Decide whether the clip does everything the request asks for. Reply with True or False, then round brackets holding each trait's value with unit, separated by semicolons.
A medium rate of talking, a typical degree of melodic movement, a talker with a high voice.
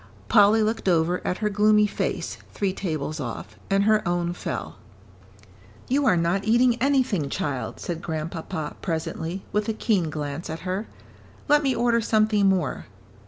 True (155 wpm; 4.8 semitones; 195 Hz)